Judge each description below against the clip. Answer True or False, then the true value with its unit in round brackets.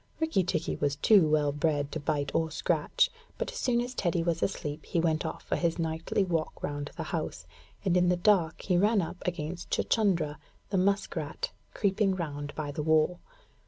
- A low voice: False (165 Hz)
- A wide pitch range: False (3.7 semitones)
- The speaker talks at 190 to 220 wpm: True (195 wpm)